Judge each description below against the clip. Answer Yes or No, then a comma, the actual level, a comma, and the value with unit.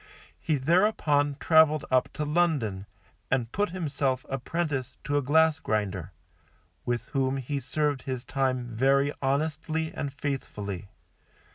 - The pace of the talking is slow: Yes, slow, 125 wpm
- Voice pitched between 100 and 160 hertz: Yes, medium, 140 Hz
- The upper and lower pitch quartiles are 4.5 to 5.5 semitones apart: No, average, 3.3 semitones